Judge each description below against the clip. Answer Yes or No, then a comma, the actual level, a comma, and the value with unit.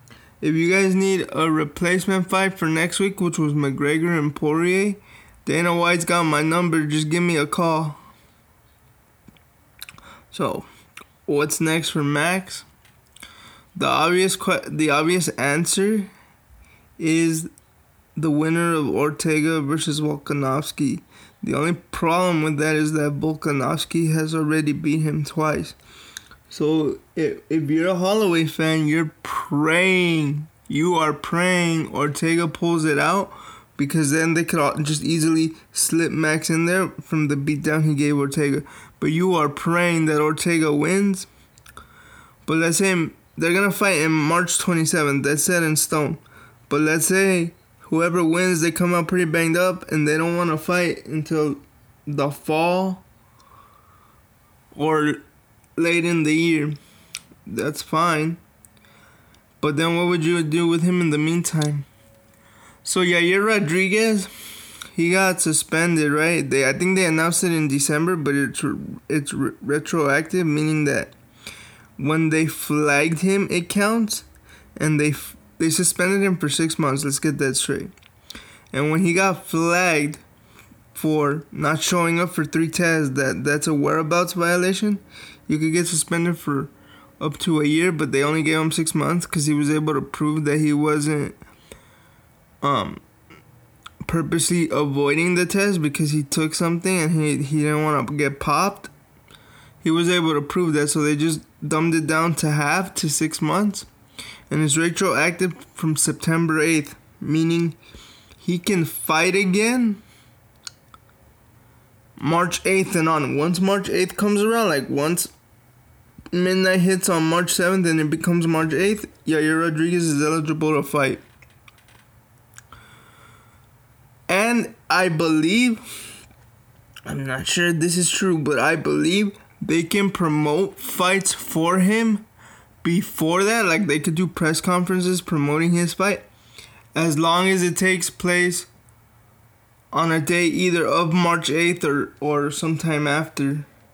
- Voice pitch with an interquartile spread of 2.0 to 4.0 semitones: Yes, average, 2.8 semitones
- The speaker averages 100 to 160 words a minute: Yes, average, 145 wpm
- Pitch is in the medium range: Yes, medium, 160 Hz